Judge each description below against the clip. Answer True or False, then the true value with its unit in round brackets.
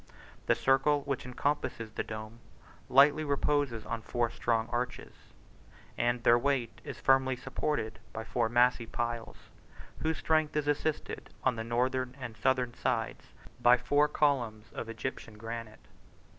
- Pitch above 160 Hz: False (125 Hz)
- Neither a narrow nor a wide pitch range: True (3.4 semitones)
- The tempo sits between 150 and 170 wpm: False (140 wpm)